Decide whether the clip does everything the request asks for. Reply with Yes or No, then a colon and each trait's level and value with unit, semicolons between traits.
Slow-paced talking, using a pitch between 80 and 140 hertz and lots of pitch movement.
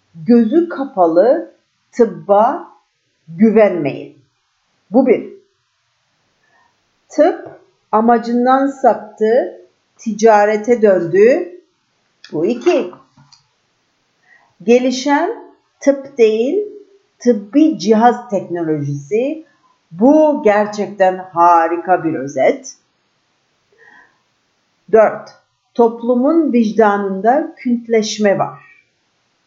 No: slow, 60 wpm; high, 235 Hz; wide, 6.1 semitones